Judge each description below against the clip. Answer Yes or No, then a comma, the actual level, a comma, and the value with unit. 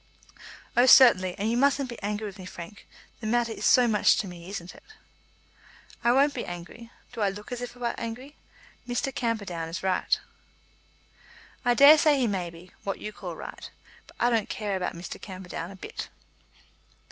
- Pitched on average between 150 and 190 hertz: No, high, 215 Hz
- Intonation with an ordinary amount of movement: Yes, average, 4.6 semitones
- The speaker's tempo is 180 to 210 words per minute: Yes, average, 185 wpm